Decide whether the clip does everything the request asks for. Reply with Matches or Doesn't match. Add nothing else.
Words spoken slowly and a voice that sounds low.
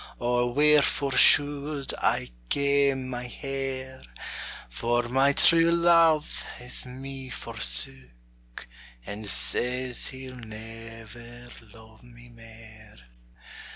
Matches